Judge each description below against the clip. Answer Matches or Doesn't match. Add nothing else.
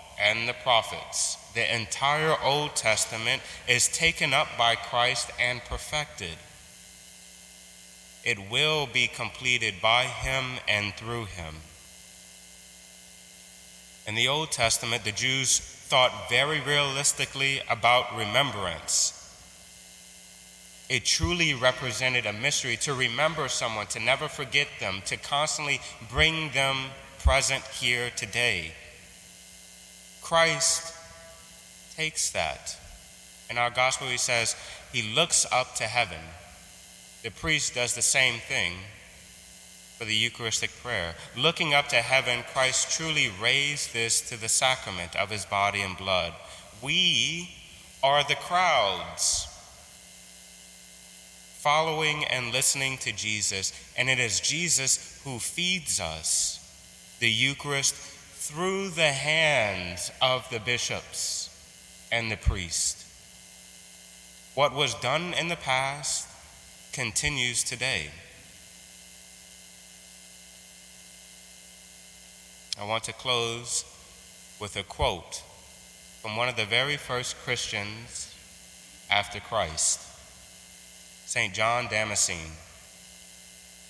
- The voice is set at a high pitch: Doesn't match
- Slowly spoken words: Matches